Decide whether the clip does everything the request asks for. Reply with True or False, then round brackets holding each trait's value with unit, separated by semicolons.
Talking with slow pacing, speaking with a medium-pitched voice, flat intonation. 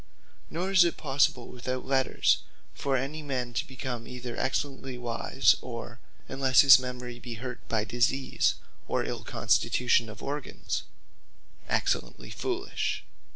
False (130 wpm; 130 Hz; 2.1 semitones)